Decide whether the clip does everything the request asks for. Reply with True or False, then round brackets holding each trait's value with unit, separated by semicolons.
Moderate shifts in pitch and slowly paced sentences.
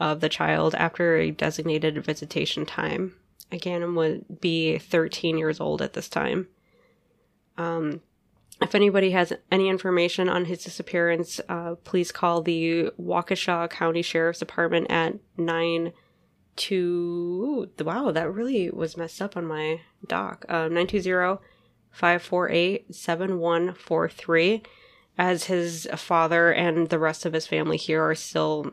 False (1.8 semitones; 125 wpm)